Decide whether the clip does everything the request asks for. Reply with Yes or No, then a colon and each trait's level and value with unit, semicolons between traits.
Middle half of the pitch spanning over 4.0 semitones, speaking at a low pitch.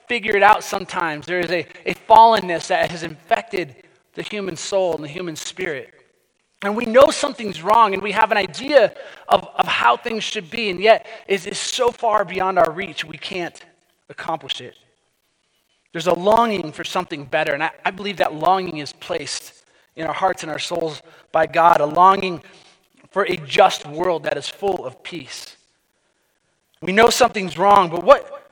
No: average, 4.5 semitones; high, 190 Hz